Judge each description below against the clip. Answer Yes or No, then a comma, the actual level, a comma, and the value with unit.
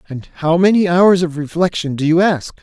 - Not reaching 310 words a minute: Yes, fast, 205 wpm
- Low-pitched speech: No, medium, 170 Hz